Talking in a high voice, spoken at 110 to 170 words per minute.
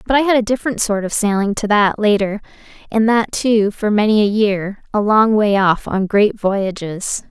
No: high, 210 Hz; fast, 205 wpm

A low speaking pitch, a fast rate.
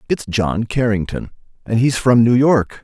No: low, 115 Hz; average, 170 wpm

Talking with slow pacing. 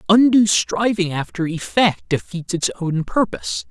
Yes: slow, 130 wpm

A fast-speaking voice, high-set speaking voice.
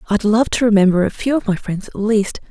Yes: fast, 265 wpm; high, 210 Hz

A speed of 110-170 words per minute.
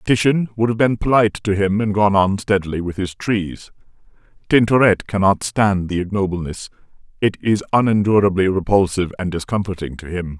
Yes: average, 155 wpm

